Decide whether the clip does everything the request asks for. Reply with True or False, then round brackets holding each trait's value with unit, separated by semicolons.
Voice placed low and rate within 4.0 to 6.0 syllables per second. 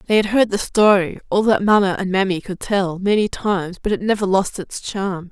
False (195 Hz; 5.2 syllables/s)